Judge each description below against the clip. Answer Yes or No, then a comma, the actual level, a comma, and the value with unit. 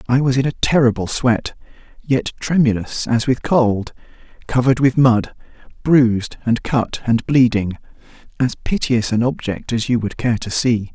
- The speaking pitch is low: Yes, low, 120 Hz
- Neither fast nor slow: Yes, average, 150 wpm